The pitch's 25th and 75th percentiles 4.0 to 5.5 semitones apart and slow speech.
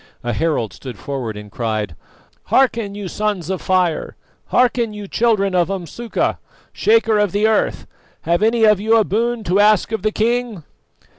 No: average, 4.7 semitones; average, 165 wpm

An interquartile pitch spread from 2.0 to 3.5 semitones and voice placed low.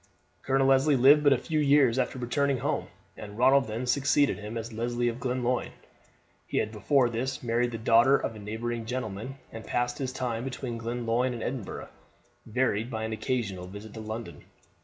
Yes: average, 2.7 semitones; low, 120 Hz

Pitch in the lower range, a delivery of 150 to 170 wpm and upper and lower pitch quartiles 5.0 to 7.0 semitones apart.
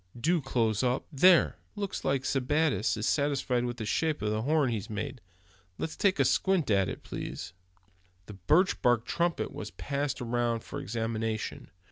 Yes: low, 125 Hz; average, 165 wpm; average, 5.3 semitones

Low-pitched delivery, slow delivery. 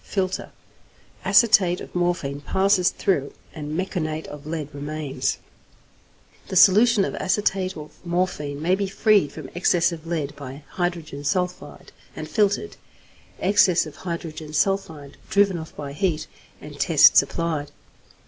No: medium, 170 Hz; slow, 130 wpm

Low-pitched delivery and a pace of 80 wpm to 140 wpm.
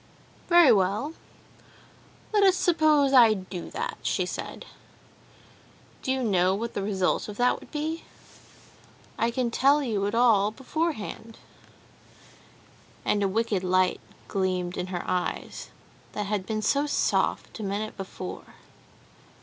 No: high, 215 Hz; slow, 135 wpm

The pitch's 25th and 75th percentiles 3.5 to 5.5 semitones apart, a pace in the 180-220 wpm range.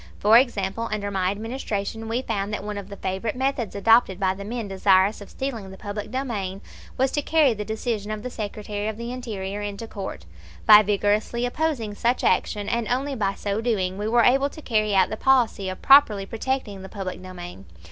No: average, 3.1 semitones; average, 200 wpm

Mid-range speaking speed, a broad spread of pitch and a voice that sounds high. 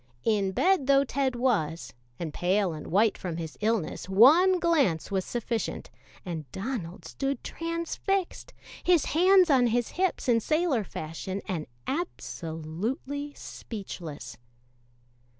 No: slow, 120 wpm; wide, 8.6 semitones; high, 230 Hz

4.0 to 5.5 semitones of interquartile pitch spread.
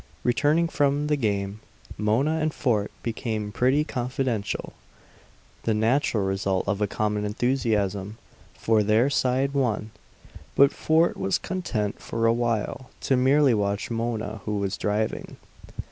Yes: average, 4.5 semitones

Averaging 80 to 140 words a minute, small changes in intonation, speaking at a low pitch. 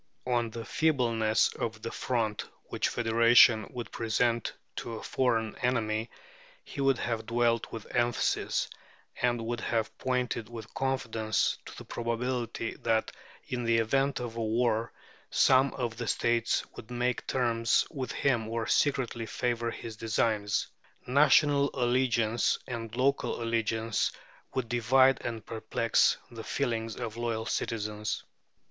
Yes: slow, 135 wpm; narrow, 1.7 semitones; low, 115 Hz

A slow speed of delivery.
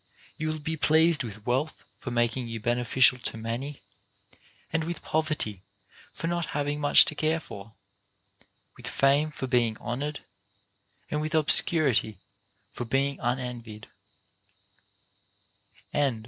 Yes: slow, 120 wpm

